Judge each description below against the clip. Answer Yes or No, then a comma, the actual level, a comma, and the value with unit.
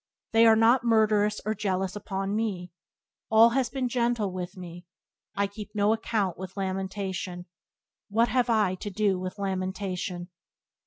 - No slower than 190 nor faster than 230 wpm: No, average, 150 wpm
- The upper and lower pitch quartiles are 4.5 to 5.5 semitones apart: No, average, 3.0 semitones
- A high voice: Yes, high, 200 Hz